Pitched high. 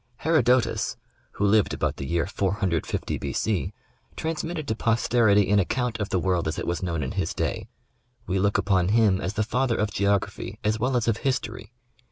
No: low, 105 Hz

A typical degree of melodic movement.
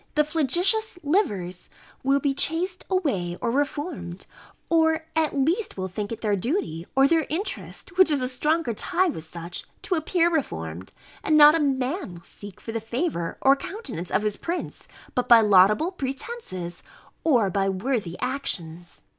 No: wide, 8.9 semitones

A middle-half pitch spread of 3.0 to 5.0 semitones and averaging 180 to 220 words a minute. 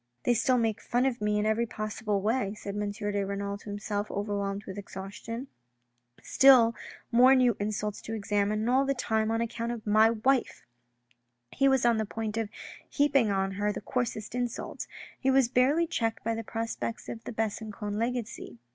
No: narrow, 2.6 semitones; average, 190 wpm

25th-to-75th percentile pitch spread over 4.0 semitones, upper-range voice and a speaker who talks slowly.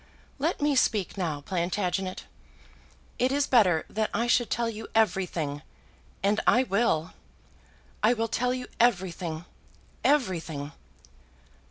Yes: wide, 5.6 semitones; high, 210 Hz; slow, 120 wpm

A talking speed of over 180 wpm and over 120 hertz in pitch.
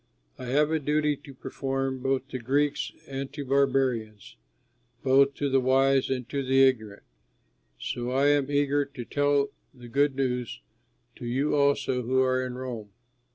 No: average, 160 wpm; low, 135 Hz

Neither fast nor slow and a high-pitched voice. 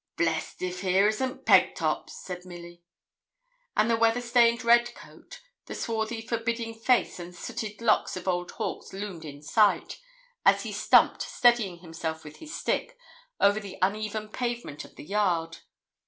Yes: average, 155 wpm; high, 210 Hz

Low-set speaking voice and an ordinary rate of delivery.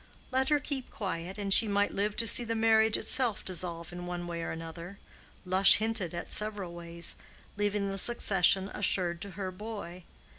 No: high, 195 Hz; average, 170 wpm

